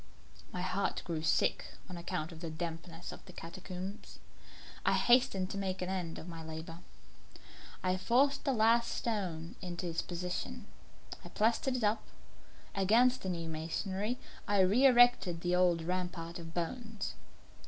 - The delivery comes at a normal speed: Yes, average, 155 wpm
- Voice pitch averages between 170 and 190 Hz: Yes, medium, 185 Hz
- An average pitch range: Yes, average, 4.3 semitones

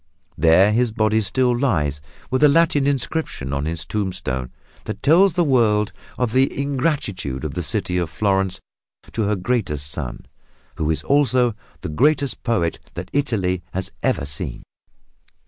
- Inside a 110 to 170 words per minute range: Yes, average, 150 wpm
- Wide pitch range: Yes, wide, 7.9 semitones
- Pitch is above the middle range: No, low, 105 Hz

